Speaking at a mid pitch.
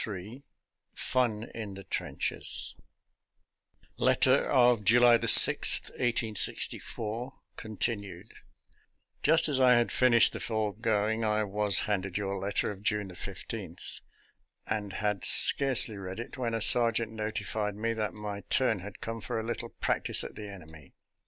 No: low, 110 Hz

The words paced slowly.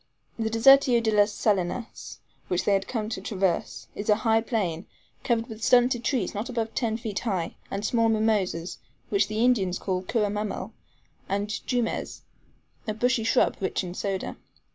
No: average, 165 wpm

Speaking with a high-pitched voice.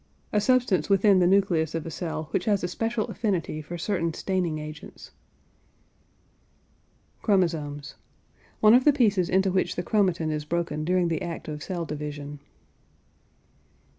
No: medium, 175 Hz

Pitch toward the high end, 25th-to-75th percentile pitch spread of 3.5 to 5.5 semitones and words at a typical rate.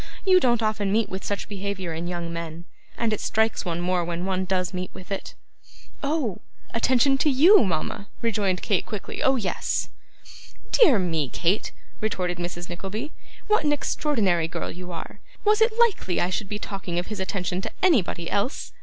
Yes: high, 195 Hz; average, 4.9 semitones; average, 180 wpm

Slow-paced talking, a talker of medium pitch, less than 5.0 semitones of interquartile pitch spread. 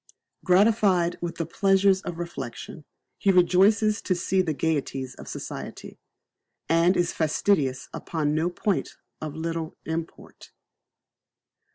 Yes: slow, 120 wpm; medium, 170 Hz; average, 3.1 semitones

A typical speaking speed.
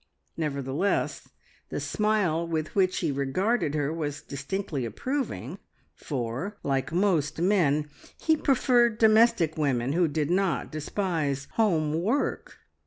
No: slow, 115 wpm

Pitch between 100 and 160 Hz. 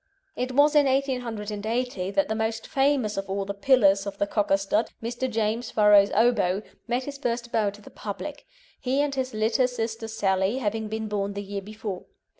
No: high, 220 Hz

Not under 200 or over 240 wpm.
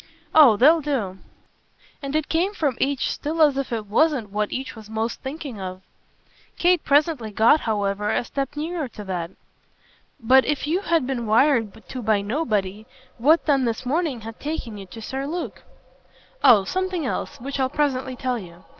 No: average, 175 wpm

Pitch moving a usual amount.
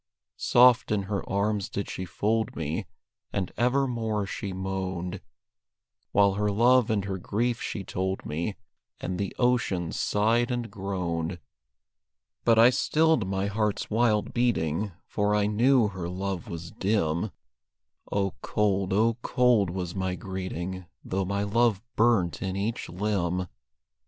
Yes: average, 3.3 semitones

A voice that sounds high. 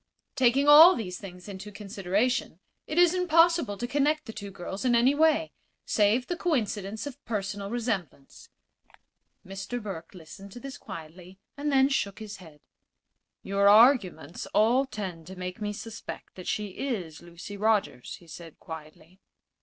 Yes: high, 205 Hz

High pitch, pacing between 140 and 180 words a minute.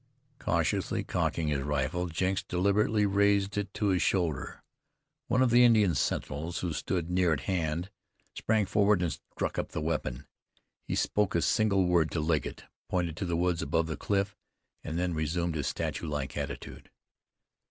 No: very low, 90 Hz; average, 165 wpm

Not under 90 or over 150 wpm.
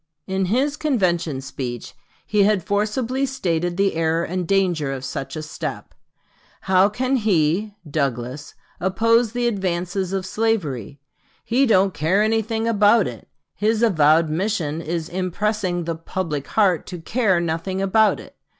Yes: average, 140 wpm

